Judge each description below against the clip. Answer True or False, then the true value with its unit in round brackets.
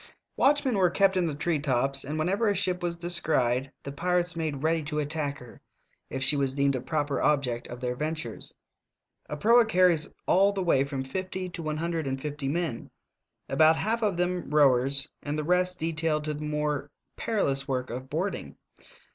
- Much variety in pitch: False (4.3 semitones)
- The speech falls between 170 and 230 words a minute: True (190 wpm)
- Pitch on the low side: False (155 Hz)